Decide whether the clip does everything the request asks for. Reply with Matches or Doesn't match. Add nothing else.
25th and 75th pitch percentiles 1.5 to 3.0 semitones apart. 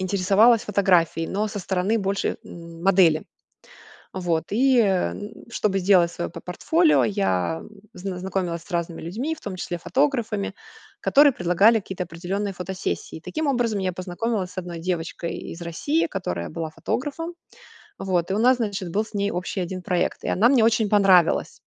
Doesn't match